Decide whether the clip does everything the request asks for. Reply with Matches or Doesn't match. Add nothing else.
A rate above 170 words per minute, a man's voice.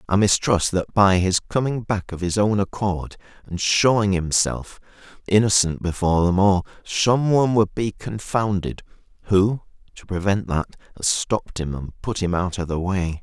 Doesn't match